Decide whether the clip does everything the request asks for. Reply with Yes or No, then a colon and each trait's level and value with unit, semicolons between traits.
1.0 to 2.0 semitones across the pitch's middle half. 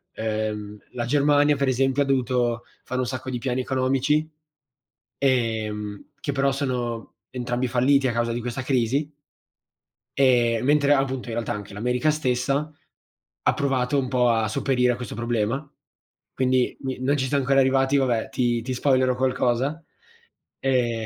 No: narrow, 2.4 semitones